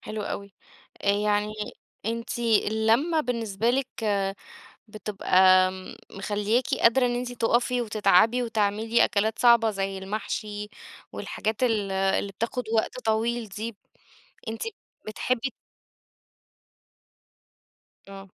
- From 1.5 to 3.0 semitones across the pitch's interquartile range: Yes, narrow, 2.6 semitones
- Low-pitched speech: No, high, 220 Hz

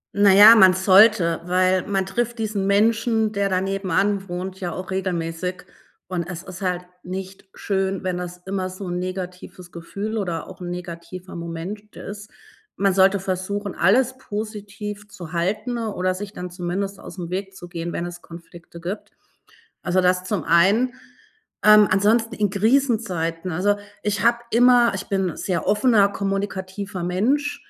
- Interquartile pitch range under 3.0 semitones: Yes, narrow, 2.4 semitones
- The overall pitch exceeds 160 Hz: Yes, high, 190 Hz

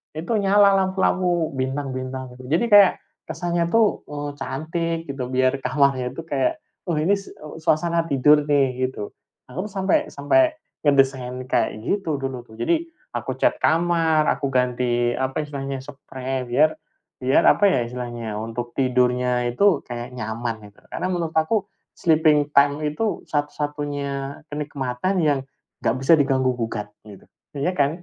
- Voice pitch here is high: No, medium, 140 Hz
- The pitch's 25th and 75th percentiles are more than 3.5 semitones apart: Yes, average, 4.5 semitones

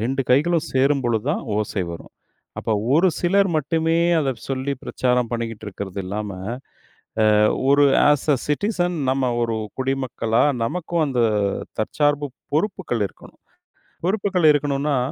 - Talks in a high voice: No, low, 135 Hz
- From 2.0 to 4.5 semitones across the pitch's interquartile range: No, average, 5.2 semitones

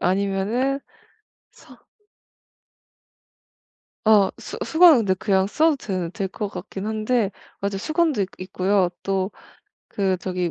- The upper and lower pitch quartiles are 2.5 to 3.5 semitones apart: Yes, average, 2.9 semitones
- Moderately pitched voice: No, high, 200 Hz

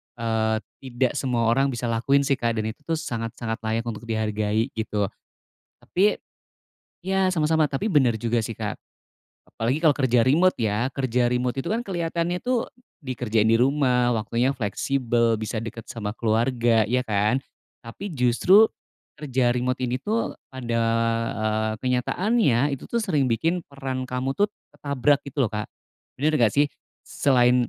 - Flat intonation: No, average, 4.0 semitones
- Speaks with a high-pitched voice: No, low, 125 Hz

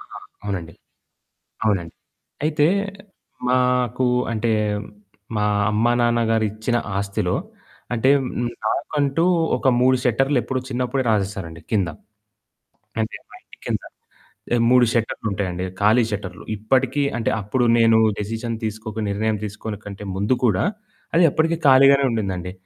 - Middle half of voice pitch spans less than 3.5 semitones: No, average, 3.9 semitones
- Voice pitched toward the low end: Yes, low, 110 Hz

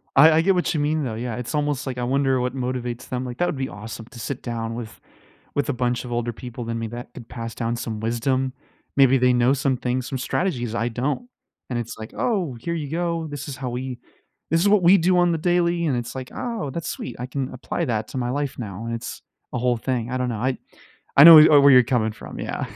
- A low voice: Yes, low, 130 Hz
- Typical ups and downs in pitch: Yes, average, 3.5 semitones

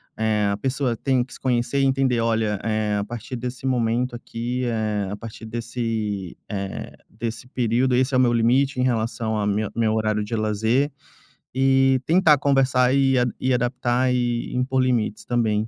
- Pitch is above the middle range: No, low, 120 Hz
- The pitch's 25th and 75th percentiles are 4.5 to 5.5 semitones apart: No, average, 2.8 semitones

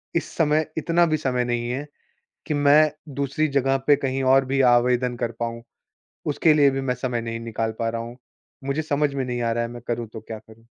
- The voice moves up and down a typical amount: Yes, average, 3.5 semitones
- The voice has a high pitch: No, low, 130 Hz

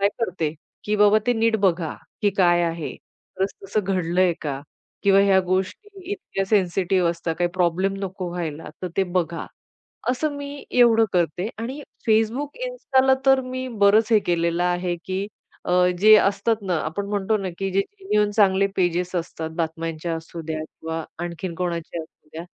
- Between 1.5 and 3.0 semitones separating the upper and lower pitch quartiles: No, average, 4.1 semitones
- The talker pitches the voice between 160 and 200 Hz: Yes, high, 190 Hz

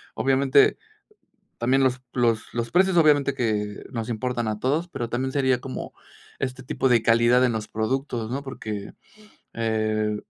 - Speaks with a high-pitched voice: No, low, 125 Hz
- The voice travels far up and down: No, average, 3.1 semitones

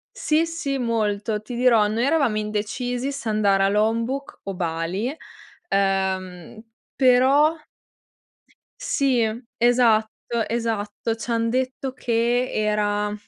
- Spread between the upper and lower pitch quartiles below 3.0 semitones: No, average, 3.4 semitones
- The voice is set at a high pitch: Yes, high, 230 Hz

